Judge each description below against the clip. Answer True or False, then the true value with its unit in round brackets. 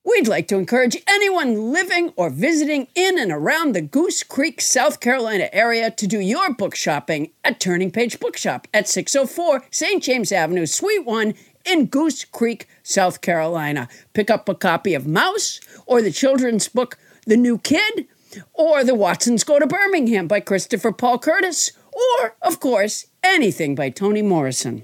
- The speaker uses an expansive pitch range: True (8.4 semitones)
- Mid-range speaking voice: False (245 Hz)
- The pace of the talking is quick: False (165 wpm)